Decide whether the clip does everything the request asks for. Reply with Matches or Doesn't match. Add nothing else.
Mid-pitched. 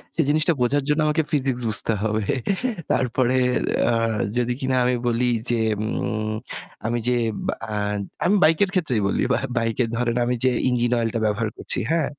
Doesn't match